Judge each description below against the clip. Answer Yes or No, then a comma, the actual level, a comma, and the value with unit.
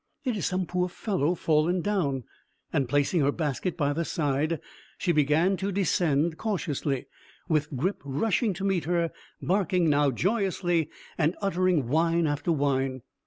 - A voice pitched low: No, medium, 165 Hz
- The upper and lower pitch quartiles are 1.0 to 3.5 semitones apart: No, average, 4.2 semitones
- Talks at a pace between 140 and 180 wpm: Yes, average, 150 wpm